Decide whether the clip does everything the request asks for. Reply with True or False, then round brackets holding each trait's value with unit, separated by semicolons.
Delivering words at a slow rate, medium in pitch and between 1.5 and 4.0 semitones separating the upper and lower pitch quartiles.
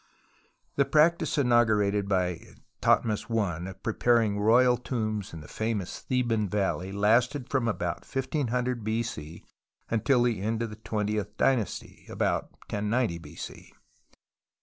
False (125 wpm; 110 Hz; 3.3 semitones)